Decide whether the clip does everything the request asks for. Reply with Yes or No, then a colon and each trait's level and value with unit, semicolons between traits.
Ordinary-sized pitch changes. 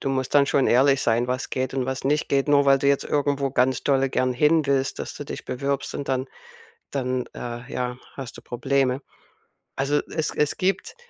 No: narrow, 1.7 semitones